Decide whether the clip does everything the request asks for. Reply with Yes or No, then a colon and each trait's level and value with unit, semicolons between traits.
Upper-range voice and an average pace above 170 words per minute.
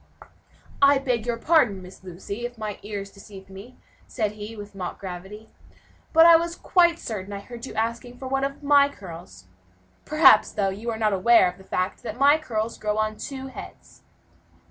Yes: high, 220 Hz; average, 190 wpm